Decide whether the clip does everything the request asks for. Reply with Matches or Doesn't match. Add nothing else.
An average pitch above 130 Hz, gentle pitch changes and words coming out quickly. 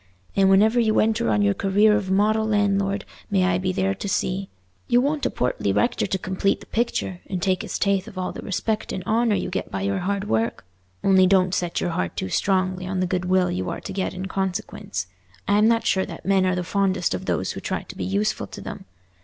Matches